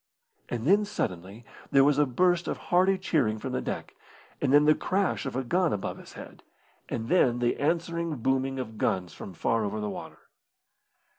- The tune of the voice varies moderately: No, wide, 7.0 semitones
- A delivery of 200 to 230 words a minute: No, average, 190 wpm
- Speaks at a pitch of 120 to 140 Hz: Yes, low, 135 Hz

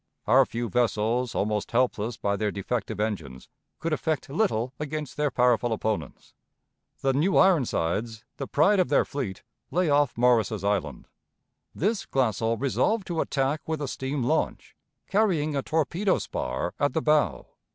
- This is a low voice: Yes, low, 130 Hz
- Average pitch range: No, wide, 5.8 semitones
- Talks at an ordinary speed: Yes, average, 150 wpm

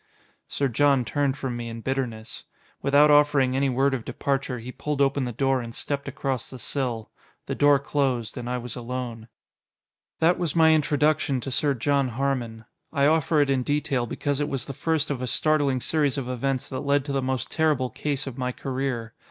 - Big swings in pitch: No, narrow, 2.4 semitones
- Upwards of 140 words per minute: Yes, average, 200 wpm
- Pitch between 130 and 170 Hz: Yes, low, 135 Hz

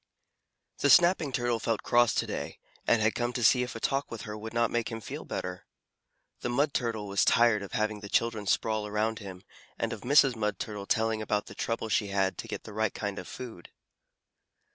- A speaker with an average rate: No, fast, 215 wpm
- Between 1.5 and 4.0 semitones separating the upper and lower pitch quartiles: Yes, narrow, 2.4 semitones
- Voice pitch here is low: Yes, low, 110 Hz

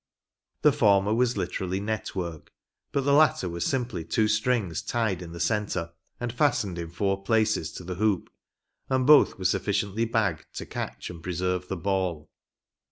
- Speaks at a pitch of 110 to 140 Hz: No, very low, 95 Hz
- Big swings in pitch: No, average, 4.1 semitones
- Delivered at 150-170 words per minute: Yes, average, 165 wpm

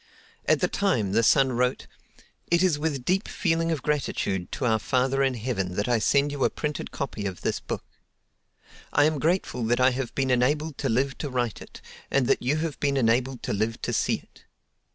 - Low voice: Yes, low, 130 Hz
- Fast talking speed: Yes, fast, 210 wpm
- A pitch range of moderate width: Yes, average, 3.7 semitones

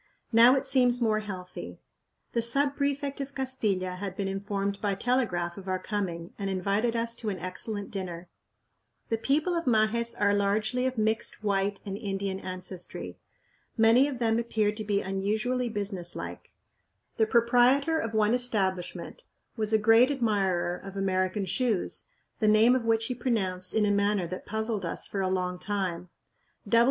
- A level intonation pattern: No, average, 3.4 semitones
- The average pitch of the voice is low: No, high, 210 Hz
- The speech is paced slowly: No, average, 165 wpm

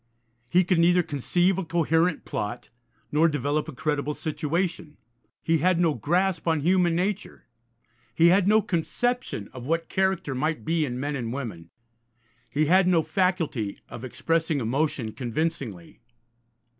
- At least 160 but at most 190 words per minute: No, average, 145 wpm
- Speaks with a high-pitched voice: No, medium, 160 Hz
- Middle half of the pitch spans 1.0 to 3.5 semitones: No, average, 4.2 semitones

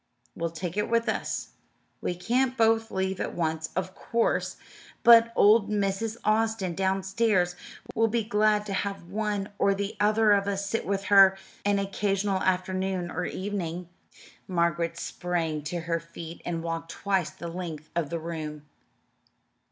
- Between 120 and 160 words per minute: Yes, average, 150 wpm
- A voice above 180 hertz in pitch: Yes, high, 190 Hz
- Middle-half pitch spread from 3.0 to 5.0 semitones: Yes, average, 3.5 semitones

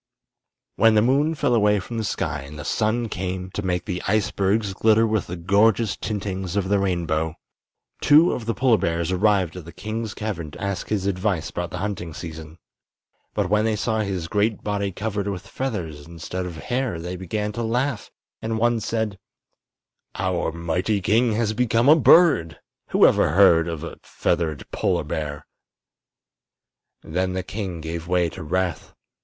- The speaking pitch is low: Yes, low, 100 Hz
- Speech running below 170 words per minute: No, average, 175 wpm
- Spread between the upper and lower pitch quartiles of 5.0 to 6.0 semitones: No, average, 4.3 semitones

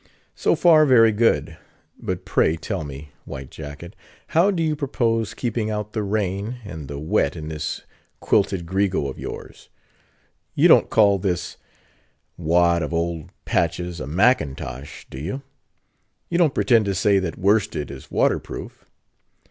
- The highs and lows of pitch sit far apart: Yes, wide, 6.1 semitones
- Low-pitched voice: Yes, very low, 95 Hz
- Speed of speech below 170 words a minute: Yes, average, 150 wpm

